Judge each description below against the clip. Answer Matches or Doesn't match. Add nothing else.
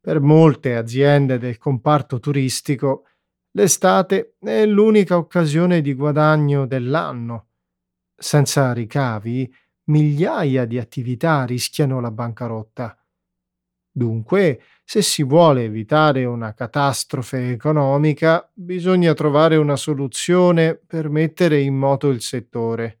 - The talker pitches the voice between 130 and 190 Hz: Matches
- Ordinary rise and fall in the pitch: Matches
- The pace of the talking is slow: Matches